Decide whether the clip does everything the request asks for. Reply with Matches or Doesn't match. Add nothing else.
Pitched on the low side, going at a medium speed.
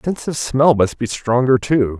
Doesn't match